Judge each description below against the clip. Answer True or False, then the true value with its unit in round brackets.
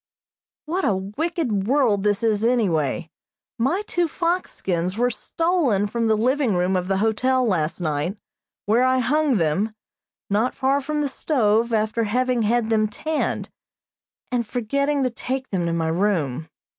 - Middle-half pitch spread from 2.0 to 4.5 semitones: False (5.1 semitones)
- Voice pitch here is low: False (225 Hz)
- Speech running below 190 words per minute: True (155 wpm)